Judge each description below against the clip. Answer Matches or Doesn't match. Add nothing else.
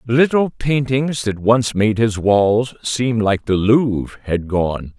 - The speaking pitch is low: Matches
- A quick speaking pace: Doesn't match